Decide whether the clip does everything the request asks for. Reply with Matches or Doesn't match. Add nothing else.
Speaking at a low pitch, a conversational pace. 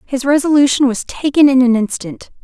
Doesn't match